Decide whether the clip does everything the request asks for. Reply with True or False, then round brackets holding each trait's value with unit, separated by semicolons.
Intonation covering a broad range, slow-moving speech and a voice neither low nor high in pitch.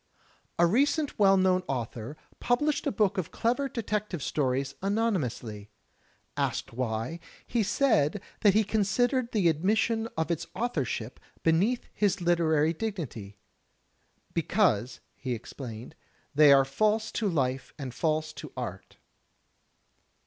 True (8.0 semitones; 120 wpm; 175 Hz)